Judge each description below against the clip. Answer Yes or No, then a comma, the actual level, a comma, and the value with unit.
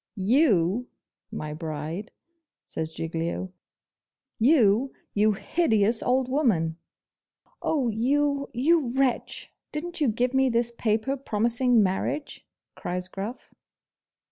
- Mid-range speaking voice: No, high, 230 Hz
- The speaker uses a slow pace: Yes, slow, 100 wpm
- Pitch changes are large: Yes, wide, 5.7 semitones